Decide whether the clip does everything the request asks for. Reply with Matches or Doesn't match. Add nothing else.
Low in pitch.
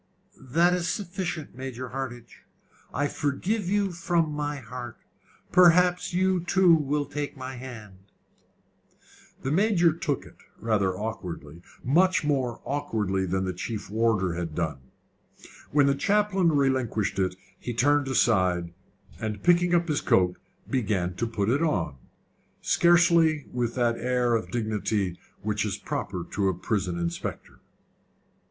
Matches